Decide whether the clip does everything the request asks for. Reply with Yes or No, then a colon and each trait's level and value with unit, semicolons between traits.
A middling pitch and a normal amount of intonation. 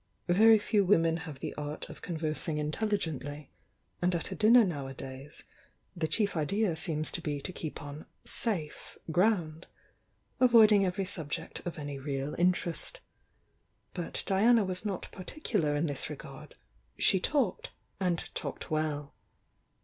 Yes: medium, 170 Hz; average, 4.9 semitones